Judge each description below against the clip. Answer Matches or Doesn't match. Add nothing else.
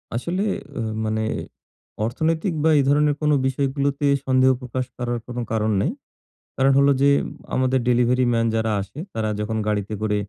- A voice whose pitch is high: Doesn't match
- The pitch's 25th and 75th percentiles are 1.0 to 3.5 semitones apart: Doesn't match